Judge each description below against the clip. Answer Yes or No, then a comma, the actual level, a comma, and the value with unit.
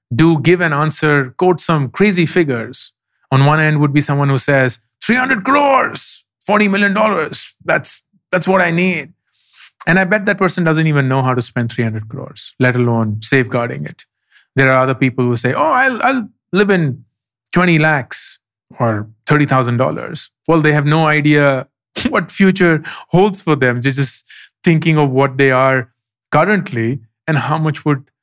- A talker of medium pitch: Yes, medium, 150 Hz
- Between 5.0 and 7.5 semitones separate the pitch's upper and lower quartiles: Yes, average, 5.3 semitones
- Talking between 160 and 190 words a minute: Yes, average, 175 wpm